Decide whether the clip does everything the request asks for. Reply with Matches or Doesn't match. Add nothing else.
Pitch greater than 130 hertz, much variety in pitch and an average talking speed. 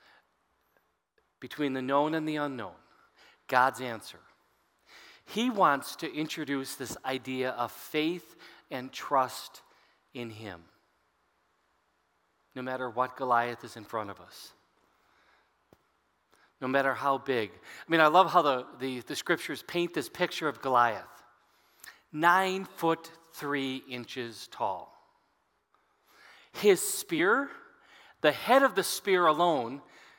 Doesn't match